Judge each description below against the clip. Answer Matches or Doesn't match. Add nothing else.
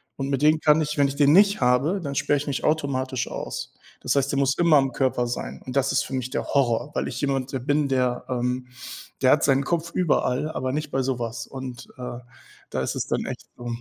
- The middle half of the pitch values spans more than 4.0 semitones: Doesn't match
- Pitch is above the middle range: Doesn't match